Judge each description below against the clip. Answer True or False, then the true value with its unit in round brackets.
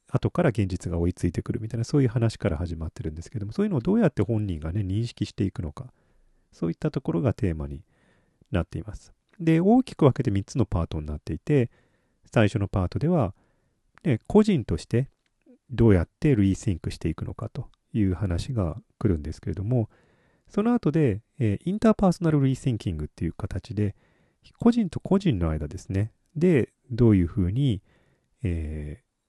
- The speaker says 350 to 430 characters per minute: True (380 characters per minute)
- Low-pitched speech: True (110 Hz)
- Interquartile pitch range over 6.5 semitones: True (6.9 semitones)